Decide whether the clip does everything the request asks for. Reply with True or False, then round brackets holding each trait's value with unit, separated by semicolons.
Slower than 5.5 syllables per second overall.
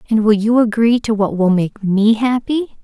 True (4.6 syllables/s)